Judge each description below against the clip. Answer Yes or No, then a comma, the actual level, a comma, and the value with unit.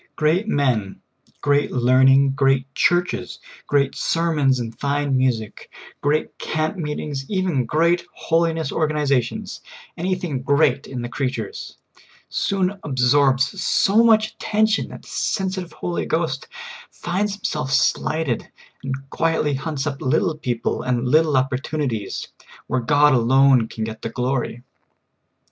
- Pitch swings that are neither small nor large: Yes, average, 4.1 semitones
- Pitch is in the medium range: Yes, medium, 145 Hz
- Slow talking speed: Yes, slow, 130 wpm